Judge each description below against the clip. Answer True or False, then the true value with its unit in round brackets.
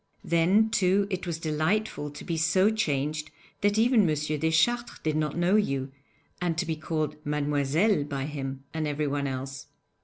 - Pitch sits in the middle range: True (155 Hz)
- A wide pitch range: False (4.3 semitones)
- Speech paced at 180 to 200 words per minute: False (160 wpm)